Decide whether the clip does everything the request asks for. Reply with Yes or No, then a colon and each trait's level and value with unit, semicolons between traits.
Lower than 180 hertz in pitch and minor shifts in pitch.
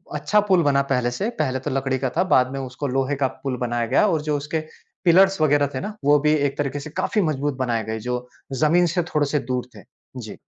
No: medium, 140 Hz; average, 3.1 semitones